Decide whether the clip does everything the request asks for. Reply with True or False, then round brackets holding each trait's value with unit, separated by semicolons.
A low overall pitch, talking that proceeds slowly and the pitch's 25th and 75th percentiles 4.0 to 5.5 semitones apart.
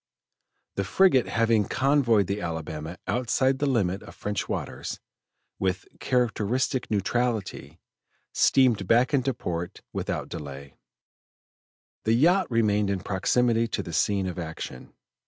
True (105 Hz; 120 wpm; 5.1 semitones)